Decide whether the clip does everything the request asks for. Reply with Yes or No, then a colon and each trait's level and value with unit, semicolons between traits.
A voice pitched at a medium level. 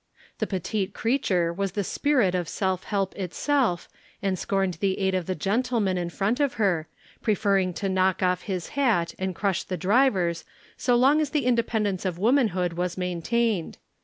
No: high, 195 Hz